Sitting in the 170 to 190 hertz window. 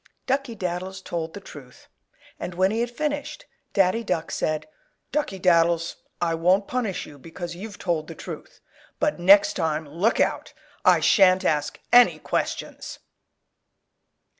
Yes: medium, 185 Hz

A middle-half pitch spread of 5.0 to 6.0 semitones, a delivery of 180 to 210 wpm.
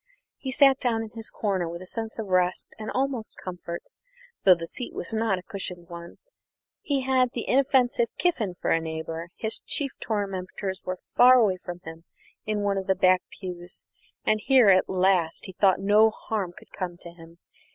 No: average, 4.2 semitones; average, 190 wpm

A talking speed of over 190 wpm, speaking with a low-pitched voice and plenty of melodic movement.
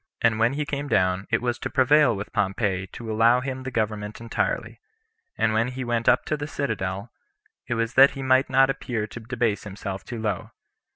No: fast, 205 wpm; low, 115 Hz; average, 3.6 semitones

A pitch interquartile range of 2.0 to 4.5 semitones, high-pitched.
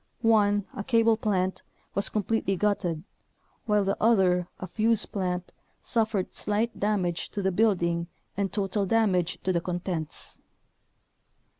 Yes: average, 3.0 semitones; high, 195 Hz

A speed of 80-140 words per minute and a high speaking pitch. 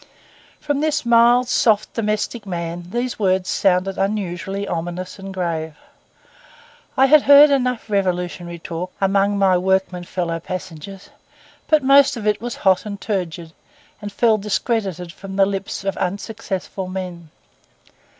Yes: slow, 135 wpm; high, 195 Hz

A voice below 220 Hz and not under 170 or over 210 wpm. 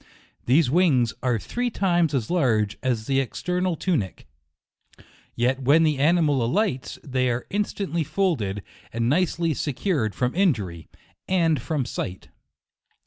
No: medium, 140 Hz; slow, 135 wpm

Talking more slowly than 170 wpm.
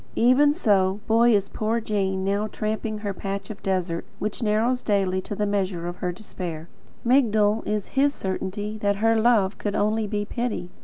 No: average, 175 wpm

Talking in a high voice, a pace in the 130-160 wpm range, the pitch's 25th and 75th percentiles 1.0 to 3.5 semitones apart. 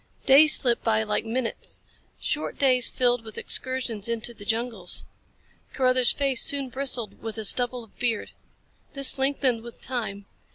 Yes: high, 245 Hz; average, 150 wpm; average, 2.7 semitones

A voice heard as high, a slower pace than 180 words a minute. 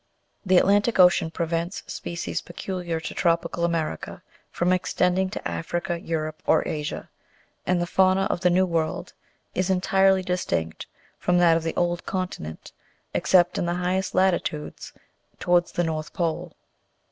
No: medium, 175 Hz; average, 145 wpm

